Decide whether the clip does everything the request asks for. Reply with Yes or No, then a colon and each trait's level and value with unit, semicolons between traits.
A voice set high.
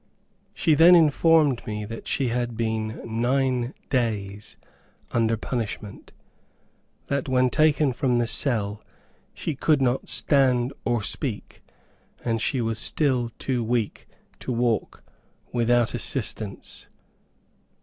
No: low, 120 Hz